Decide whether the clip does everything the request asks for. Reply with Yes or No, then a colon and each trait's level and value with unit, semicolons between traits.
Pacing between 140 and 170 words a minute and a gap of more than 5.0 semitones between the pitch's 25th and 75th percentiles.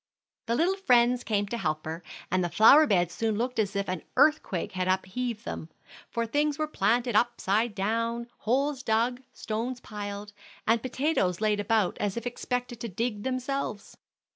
No: average, 165 wpm; average, 3.5 semitones